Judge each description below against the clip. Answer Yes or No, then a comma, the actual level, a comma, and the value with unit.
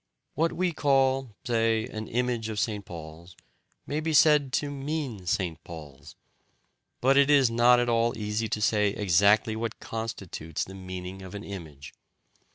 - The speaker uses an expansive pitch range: Yes, wide, 5.7 semitones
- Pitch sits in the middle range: No, low, 110 Hz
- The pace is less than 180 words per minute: Yes, average, 160 wpm